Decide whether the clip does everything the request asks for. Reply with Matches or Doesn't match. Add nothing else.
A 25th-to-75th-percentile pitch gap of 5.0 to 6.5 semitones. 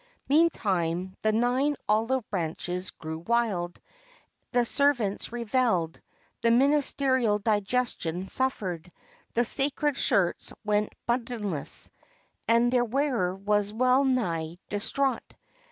Matches